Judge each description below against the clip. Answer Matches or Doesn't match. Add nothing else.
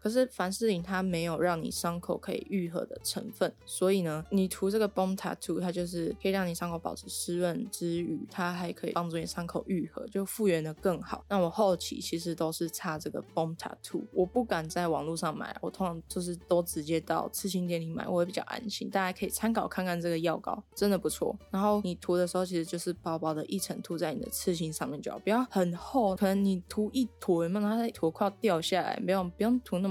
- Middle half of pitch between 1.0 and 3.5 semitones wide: Matches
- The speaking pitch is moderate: Matches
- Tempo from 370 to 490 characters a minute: Matches